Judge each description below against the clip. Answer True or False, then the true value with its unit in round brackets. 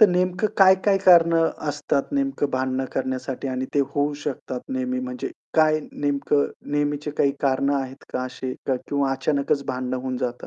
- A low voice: False (145 Hz)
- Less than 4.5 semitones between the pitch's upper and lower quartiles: False (4.8 semitones)